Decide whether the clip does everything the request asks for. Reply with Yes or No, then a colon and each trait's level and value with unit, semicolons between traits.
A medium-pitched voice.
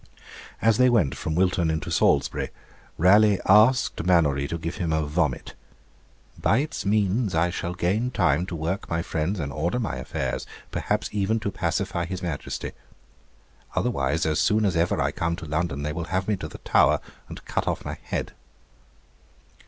No: very low, 90 Hz